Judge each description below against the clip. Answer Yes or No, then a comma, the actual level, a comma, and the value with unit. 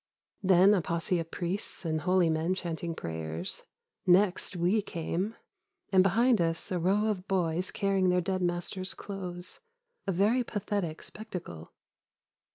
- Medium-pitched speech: Yes, medium, 180 Hz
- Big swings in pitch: No, average, 2.7 semitones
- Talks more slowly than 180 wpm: Yes, average, 140 wpm